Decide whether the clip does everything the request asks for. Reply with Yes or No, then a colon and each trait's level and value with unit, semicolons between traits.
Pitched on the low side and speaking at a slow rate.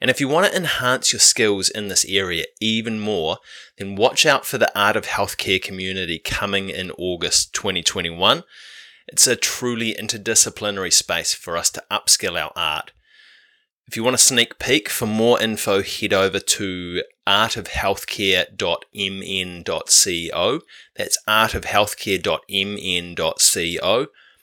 Yes: low, 100 Hz; slow, 130 wpm